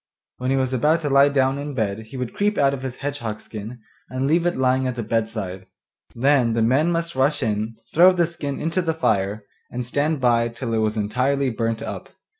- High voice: No, low, 130 Hz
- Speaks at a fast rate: Yes, fast, 220 wpm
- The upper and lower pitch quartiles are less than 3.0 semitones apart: No, average, 4.1 semitones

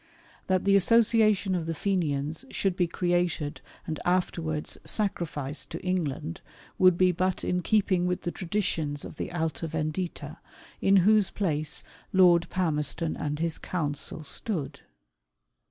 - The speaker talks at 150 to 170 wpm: No, slow, 135 wpm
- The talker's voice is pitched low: No, medium, 175 Hz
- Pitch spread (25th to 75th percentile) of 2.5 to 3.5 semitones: Yes, average, 3.2 semitones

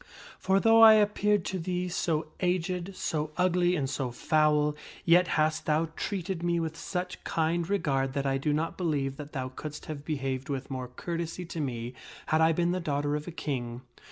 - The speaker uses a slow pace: No, average, 190 wpm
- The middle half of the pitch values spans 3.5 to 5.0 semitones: Yes, average, 4.0 semitones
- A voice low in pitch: No, medium, 160 Hz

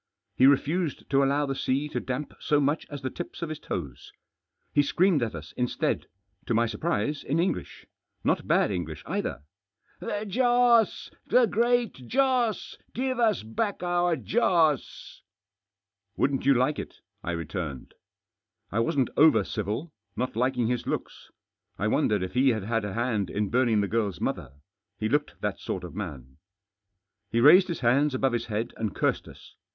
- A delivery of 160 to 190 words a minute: Yes, average, 180 wpm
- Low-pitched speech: Yes, low, 130 Hz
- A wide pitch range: Yes, wide, 7.8 semitones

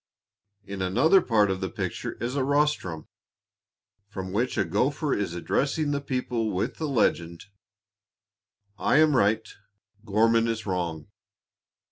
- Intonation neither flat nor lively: No, wide, 6.5 semitones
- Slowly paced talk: Yes, slow, 130 wpm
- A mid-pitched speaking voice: No, low, 115 Hz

